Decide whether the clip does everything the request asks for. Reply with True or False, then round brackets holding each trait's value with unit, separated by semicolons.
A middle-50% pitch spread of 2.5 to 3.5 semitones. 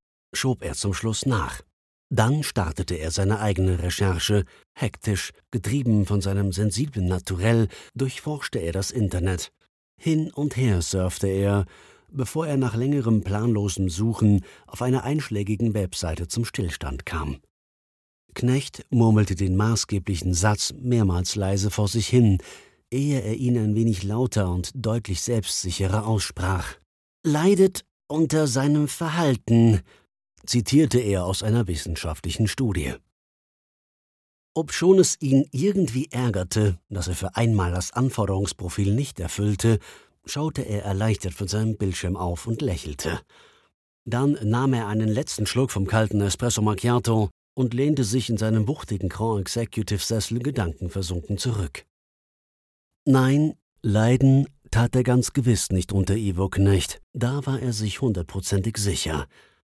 False (4.6 semitones)